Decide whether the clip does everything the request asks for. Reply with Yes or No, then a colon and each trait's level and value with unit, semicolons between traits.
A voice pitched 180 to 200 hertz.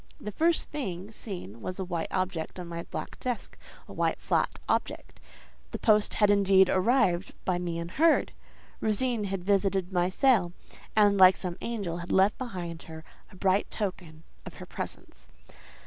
Yes: high, 190 Hz